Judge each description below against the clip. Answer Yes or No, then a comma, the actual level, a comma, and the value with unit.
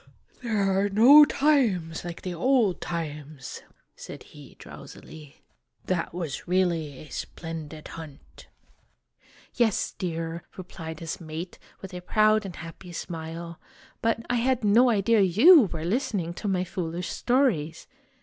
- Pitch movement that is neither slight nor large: Yes, average, 4.9 semitones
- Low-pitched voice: No, medium, 180 Hz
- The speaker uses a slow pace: Yes, slow, 130 wpm